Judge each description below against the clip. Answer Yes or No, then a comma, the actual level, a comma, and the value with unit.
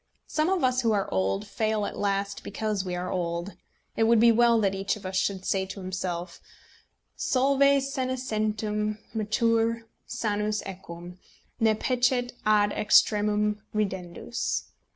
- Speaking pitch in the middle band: No, high, 210 Hz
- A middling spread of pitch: Yes, average, 3.3 semitones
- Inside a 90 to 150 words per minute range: Yes, average, 140 wpm